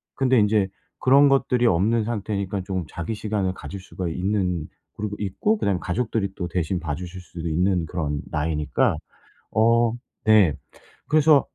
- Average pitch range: Yes, average, 4.2 semitones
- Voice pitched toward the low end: Yes, low, 100 Hz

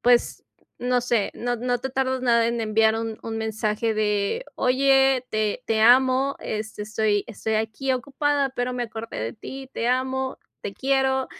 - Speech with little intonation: No, average, 3.1 semitones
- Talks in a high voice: Yes, high, 245 Hz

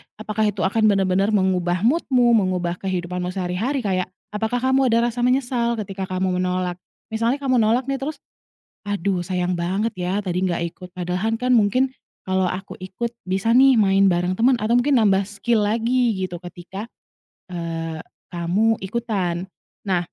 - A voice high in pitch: Yes, high, 195 Hz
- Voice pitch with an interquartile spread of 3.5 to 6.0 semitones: Yes, average, 4.4 semitones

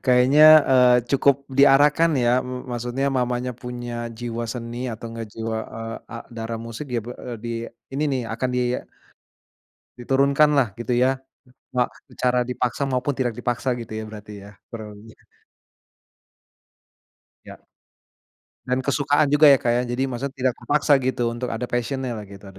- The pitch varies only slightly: Yes, narrow, 2.3 semitones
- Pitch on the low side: Yes, low, 125 Hz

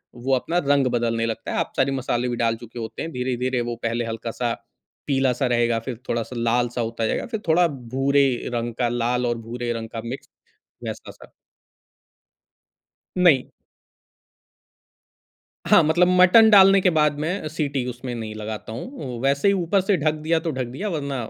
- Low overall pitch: Yes, low, 125 Hz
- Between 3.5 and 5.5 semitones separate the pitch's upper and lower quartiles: Yes, average, 4.6 semitones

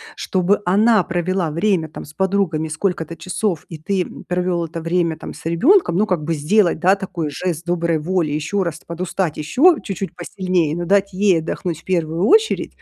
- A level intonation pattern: No, average, 3.0 semitones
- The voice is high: No, medium, 175 Hz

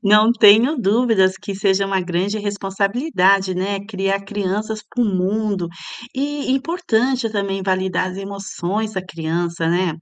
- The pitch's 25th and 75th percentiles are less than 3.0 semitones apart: Yes, narrow, 2.6 semitones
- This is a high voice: Yes, high, 200 Hz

